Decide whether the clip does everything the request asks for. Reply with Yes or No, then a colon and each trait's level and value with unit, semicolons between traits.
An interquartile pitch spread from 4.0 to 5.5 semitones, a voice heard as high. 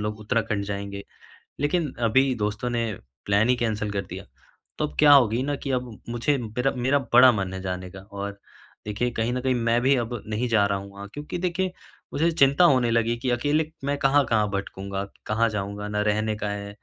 No: average, 4.8 semitones; low, 115 Hz